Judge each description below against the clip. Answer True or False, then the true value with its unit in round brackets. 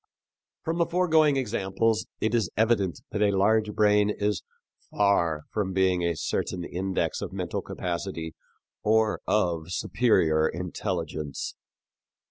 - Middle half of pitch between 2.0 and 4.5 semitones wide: True (4.0 semitones)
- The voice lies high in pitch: False (100 Hz)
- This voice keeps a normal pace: False (120 wpm)